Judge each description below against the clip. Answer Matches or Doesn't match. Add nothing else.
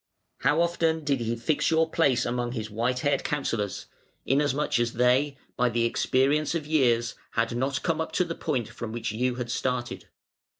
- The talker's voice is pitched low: Matches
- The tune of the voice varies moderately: Matches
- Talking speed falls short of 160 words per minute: Doesn't match